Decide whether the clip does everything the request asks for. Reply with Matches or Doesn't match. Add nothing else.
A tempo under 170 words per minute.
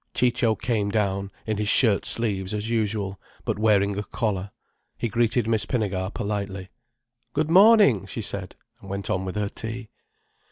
Matches